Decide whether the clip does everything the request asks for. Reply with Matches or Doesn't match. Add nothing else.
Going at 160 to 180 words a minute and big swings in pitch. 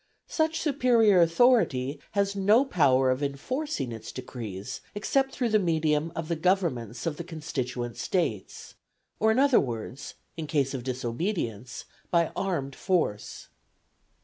Doesn't match